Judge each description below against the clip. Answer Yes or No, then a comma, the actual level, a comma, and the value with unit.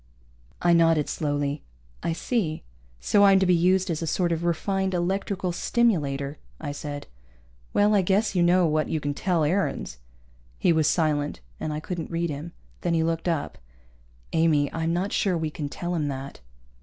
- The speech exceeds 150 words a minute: Yes, average, 180 wpm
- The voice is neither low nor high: Yes, medium, 165 Hz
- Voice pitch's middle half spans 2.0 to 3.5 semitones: Yes, average, 3.1 semitones